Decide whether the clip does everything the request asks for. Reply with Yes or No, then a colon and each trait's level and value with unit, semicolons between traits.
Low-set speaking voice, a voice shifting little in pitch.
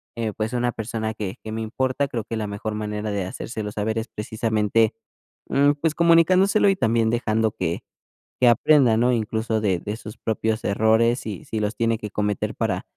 Yes: low, 110 Hz; narrow, 2.1 semitones